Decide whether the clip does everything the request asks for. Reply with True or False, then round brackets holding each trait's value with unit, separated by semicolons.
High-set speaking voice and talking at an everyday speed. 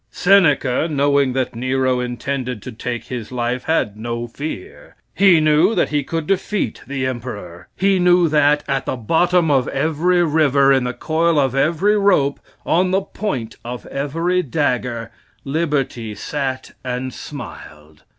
False (140 Hz; 150 wpm)